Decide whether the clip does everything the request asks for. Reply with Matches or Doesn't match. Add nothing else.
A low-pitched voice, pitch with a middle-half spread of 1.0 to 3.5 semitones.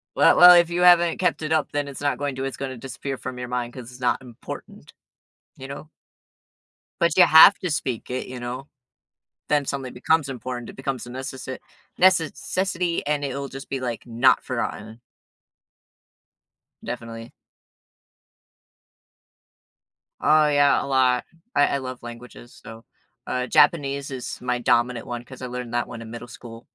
Matches